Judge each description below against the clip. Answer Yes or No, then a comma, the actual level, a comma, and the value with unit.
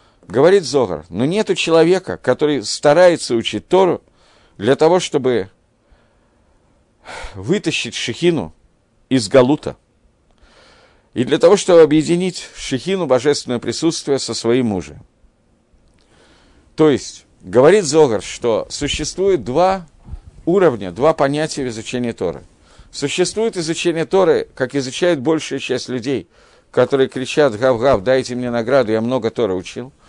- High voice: No, medium, 140 Hz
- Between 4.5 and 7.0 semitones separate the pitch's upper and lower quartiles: Yes, average, 5.2 semitones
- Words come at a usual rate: Yes, average, 120 wpm